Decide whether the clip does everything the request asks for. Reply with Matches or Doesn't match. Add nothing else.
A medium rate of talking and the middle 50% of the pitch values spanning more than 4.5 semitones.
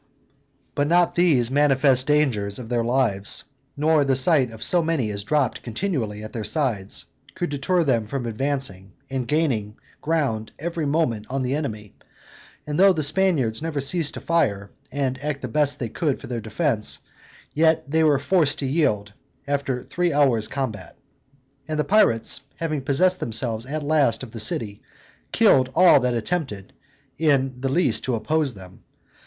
Matches